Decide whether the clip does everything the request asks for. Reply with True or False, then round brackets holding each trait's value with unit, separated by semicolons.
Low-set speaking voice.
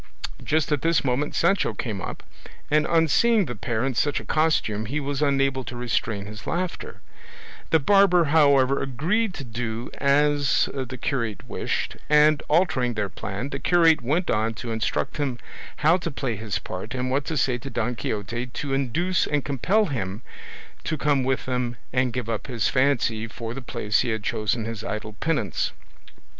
True (130 Hz)